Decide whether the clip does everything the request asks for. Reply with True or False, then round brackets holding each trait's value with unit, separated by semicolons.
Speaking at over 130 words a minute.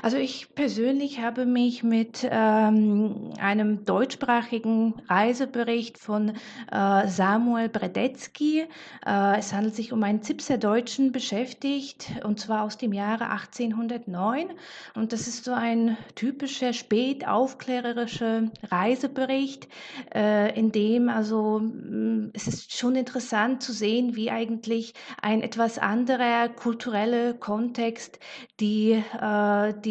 False (115 wpm)